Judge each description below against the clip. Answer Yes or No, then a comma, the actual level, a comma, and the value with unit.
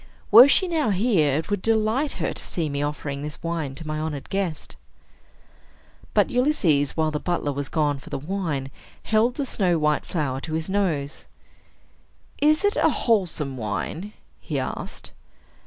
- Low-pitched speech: No, medium, 160 Hz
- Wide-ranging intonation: Yes, wide, 6.6 semitones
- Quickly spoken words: No, average, 165 wpm